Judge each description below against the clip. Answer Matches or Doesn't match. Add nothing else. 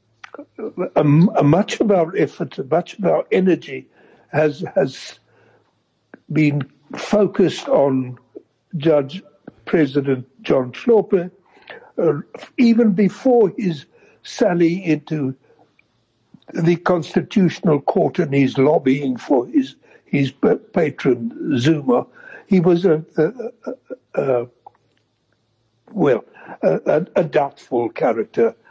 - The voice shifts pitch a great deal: Matches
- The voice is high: Doesn't match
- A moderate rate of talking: Doesn't match